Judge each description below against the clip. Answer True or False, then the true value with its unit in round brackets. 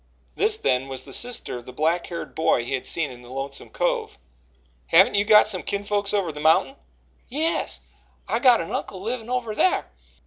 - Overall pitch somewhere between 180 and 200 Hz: True (185 Hz)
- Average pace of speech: True (195 wpm)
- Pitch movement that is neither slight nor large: False (8.7 semitones)